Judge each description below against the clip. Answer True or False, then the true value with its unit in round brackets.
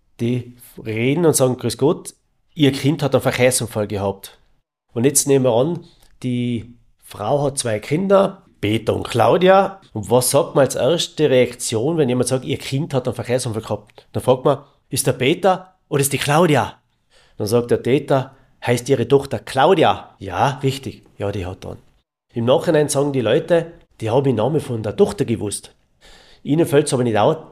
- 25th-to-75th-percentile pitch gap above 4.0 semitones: False (3.6 semitones)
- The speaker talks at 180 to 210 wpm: True (185 wpm)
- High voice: False (130 Hz)